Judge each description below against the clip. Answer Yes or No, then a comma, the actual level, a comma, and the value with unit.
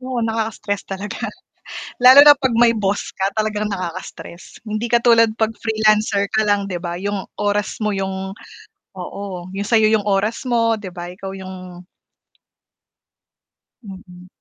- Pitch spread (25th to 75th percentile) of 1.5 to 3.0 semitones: Yes, narrow, 2.6 semitones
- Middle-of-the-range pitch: No, high, 205 Hz